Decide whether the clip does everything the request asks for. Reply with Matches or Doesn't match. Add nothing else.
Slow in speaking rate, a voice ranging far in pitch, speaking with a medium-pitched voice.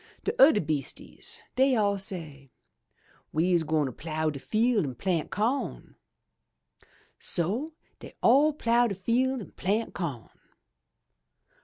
Doesn't match